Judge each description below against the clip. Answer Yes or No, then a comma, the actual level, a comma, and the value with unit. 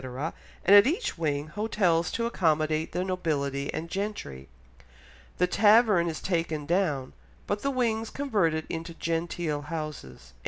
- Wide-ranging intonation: No, average, 4.9 semitones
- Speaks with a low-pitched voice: No, medium, 165 Hz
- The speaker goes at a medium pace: No, slow, 130 wpm